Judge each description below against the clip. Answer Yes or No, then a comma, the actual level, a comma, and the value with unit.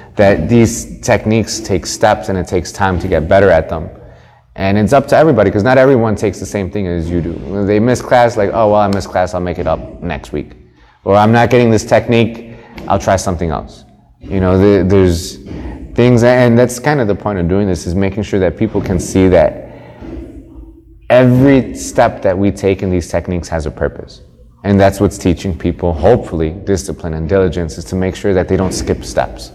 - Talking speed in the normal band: No, fast, 215 wpm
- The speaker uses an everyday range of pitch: Yes, average, 3.8 semitones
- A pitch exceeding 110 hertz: No, very low, 95 Hz